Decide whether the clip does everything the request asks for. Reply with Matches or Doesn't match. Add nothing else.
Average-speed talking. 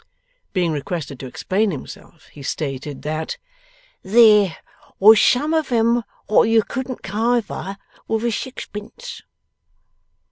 Doesn't match